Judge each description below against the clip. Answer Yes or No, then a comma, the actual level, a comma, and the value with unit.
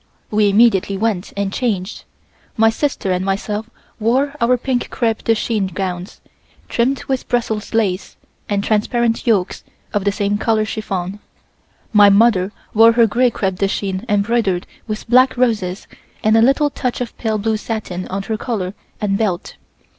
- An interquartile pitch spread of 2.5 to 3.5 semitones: Yes, average, 2.9 semitones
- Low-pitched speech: No, high, 215 Hz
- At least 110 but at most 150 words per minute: No, average, 160 wpm